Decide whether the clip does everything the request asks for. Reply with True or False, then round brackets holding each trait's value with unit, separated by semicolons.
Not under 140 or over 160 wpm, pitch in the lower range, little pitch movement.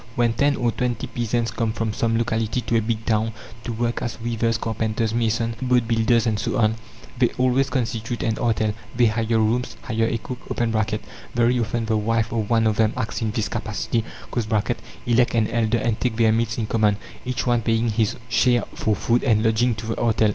False (200 wpm; 115 Hz; 1.3 semitones)